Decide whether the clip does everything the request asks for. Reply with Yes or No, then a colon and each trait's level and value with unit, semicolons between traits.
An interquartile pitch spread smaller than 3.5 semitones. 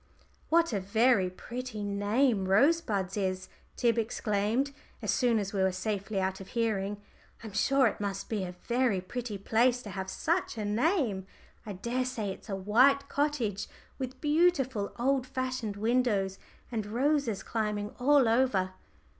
No: average, 4.3 semitones